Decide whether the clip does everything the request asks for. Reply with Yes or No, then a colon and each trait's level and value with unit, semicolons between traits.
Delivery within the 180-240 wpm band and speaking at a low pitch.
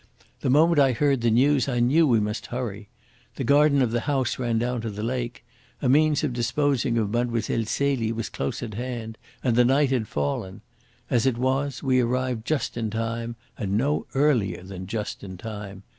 Yes: average, 195 wpm; low, 120 Hz